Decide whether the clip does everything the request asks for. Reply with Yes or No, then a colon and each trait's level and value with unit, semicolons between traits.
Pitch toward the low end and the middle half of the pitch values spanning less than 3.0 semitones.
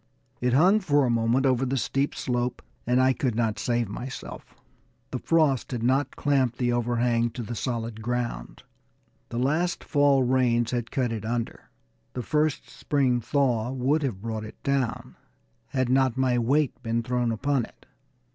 Yes: low, 125 Hz; narrow, 2.4 semitones